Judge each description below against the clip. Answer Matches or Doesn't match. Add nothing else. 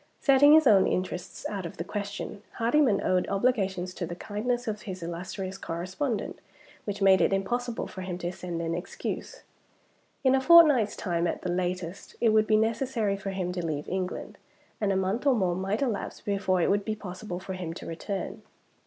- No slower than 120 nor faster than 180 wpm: Doesn't match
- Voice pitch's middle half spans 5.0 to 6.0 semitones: Doesn't match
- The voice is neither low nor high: Doesn't match